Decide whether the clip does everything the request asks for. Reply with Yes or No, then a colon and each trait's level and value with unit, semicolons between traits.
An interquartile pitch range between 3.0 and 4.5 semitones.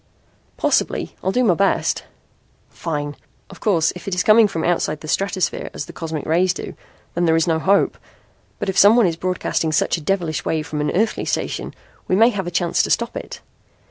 Yes: average, 3.4 semitones